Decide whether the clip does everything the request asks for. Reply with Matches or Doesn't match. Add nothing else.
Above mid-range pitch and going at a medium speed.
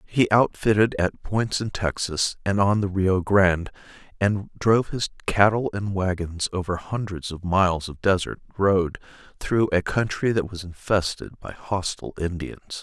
Doesn't match